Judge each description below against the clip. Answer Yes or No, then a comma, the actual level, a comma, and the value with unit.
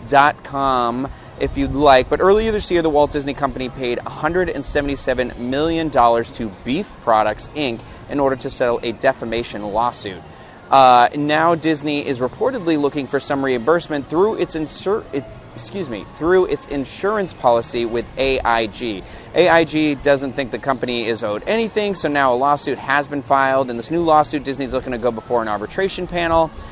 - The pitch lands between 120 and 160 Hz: Yes, medium, 140 Hz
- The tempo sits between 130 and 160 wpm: No, average, 170 wpm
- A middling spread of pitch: Yes, average, 4.0 semitones